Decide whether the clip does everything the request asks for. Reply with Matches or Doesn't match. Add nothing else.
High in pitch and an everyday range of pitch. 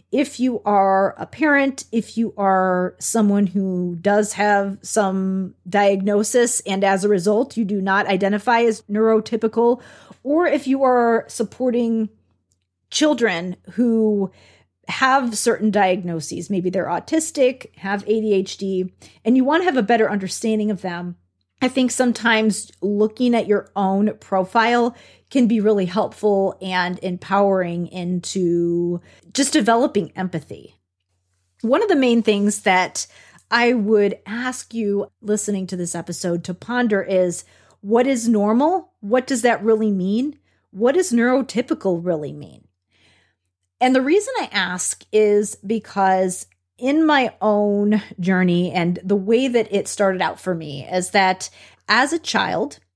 Matches